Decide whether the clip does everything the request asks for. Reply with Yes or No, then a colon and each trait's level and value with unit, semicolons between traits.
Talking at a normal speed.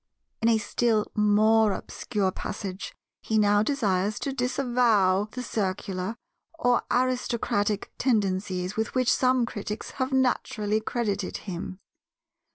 No: slow, 115 wpm